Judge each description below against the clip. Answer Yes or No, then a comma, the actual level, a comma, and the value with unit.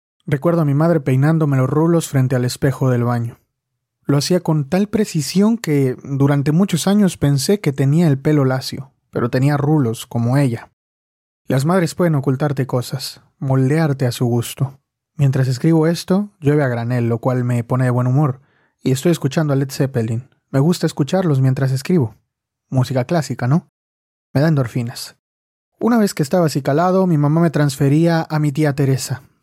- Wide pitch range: No, average, 3.8 semitones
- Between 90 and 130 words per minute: No, average, 175 wpm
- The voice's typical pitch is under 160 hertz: Yes, medium, 140 Hz